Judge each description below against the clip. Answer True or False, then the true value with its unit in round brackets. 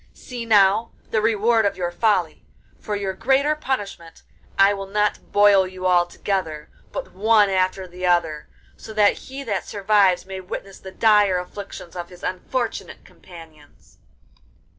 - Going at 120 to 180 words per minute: True (150 wpm)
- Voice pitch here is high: True (195 Hz)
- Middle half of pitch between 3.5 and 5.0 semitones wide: False (2.9 semitones)